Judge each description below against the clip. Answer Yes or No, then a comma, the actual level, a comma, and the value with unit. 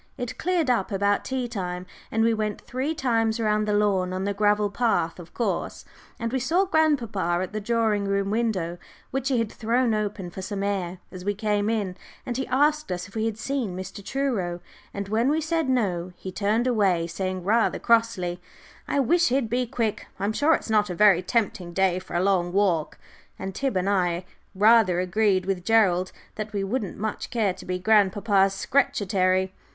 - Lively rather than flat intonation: No, average, 3.8 semitones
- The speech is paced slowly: No, average, 195 wpm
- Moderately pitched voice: No, high, 210 Hz